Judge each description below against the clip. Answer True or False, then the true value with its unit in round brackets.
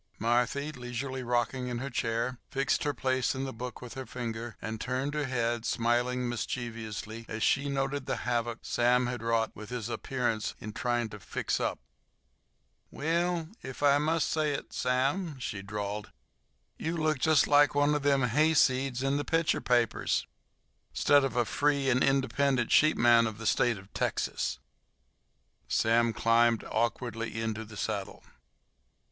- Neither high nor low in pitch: False (125 Hz)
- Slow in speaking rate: False (155 wpm)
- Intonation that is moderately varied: True (3.2 semitones)